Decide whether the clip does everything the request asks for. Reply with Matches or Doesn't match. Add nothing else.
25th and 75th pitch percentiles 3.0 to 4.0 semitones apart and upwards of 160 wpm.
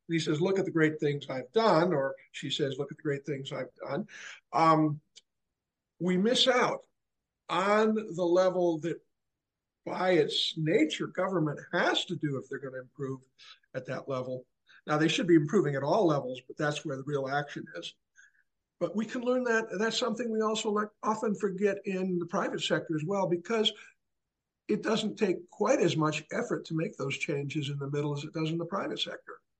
Doesn't match